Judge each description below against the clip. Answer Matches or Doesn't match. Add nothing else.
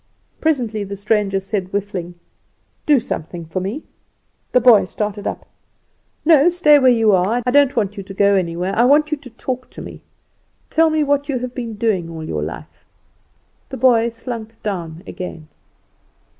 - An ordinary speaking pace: Matches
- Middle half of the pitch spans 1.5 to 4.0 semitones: Doesn't match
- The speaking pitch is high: Matches